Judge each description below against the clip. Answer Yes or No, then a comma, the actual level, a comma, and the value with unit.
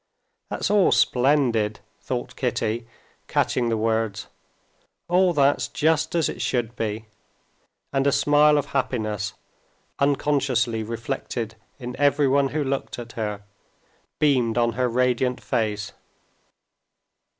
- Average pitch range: Yes, average, 3.9 semitones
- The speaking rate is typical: No, slow, 115 wpm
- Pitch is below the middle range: Yes, low, 125 Hz